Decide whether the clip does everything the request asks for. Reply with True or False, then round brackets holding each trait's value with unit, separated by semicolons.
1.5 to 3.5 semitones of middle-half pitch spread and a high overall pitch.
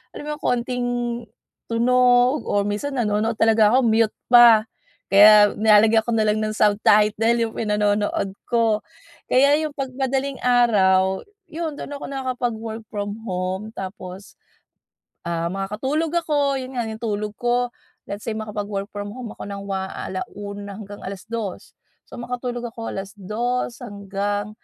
True (3.2 semitones; 220 Hz)